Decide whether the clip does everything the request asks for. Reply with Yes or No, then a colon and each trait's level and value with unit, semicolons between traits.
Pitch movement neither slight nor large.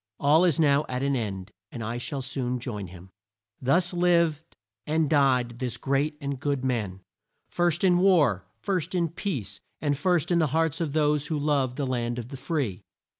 Yes: average, 4.7 semitones